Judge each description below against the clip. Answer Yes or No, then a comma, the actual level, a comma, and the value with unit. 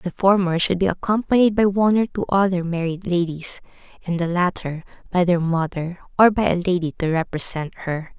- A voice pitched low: No, medium, 180 Hz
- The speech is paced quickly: No, average, 185 wpm